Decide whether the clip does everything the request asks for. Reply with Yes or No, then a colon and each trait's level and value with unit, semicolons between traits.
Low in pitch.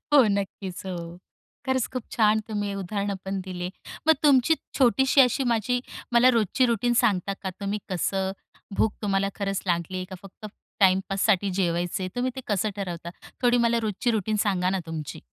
No: high, 200 Hz